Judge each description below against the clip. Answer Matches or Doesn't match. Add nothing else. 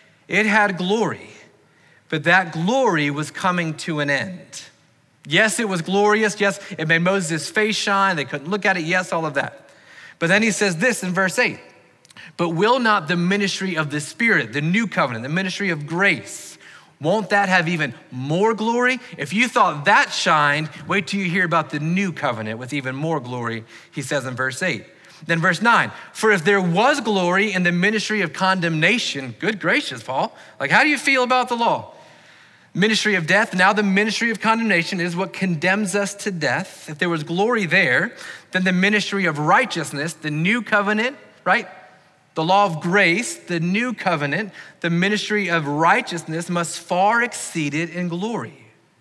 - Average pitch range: Matches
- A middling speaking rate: Matches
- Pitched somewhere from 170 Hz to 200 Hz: Matches